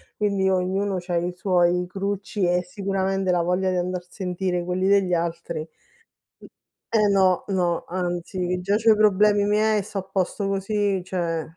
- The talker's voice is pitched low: No, high, 190 Hz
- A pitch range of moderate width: No, narrow, 1.9 semitones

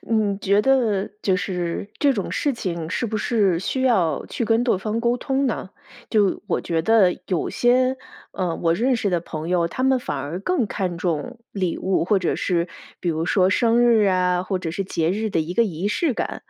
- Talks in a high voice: Yes, high, 195 Hz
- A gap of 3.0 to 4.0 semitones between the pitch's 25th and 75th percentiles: No, average, 4.9 semitones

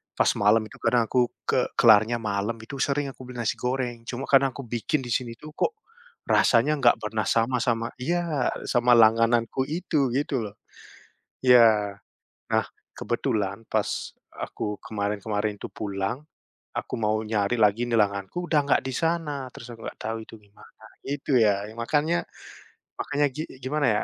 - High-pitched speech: No, low, 120 Hz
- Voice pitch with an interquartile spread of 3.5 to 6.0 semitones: Yes, average, 3.9 semitones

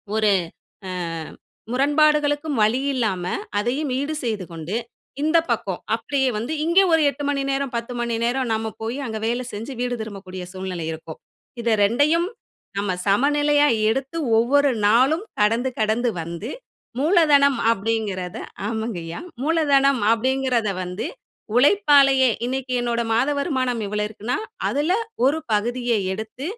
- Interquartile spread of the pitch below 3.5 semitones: No, average, 4.5 semitones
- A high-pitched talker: Yes, high, 245 Hz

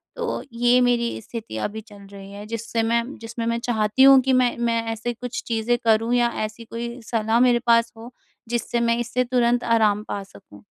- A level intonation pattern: Yes, narrow, 1.5 semitones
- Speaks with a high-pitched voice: Yes, high, 235 Hz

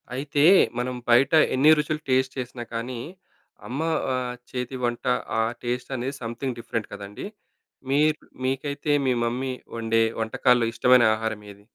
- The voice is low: Yes, low, 125 Hz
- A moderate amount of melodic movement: No, narrow, 2.3 semitones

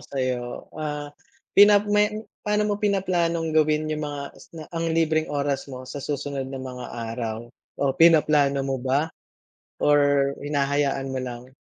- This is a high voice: No, medium, 145 Hz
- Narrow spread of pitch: No, average, 3.1 semitones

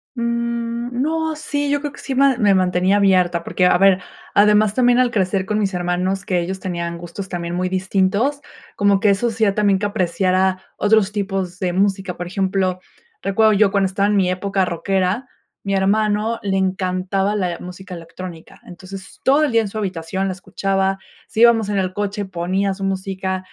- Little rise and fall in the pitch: Yes, narrow, 2.3 semitones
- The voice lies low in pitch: No, high, 195 Hz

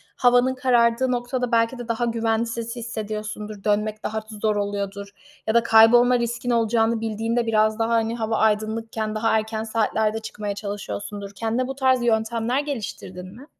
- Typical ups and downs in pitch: No, narrow, 1.7 semitones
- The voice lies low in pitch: No, high, 225 Hz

